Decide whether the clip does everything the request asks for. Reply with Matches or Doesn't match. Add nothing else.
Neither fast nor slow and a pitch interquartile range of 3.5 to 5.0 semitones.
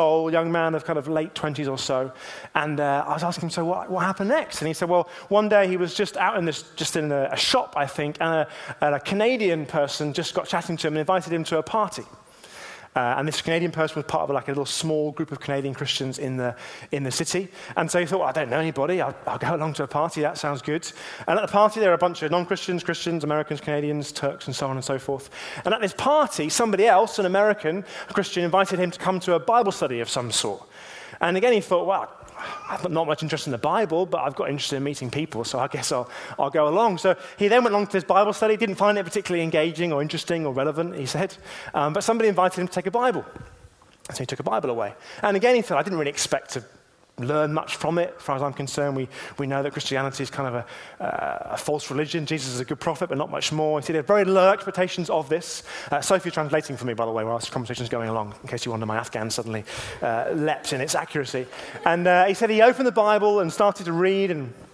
Doesn't match